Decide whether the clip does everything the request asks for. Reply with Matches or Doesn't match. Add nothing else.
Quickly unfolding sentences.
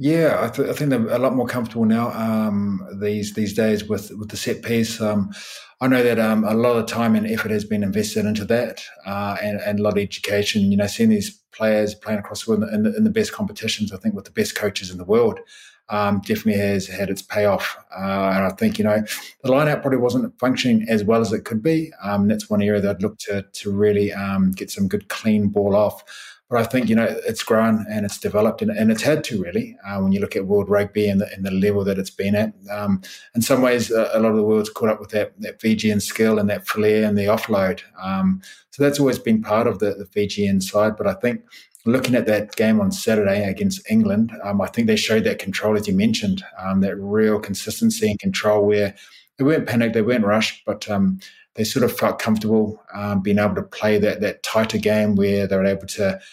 Matches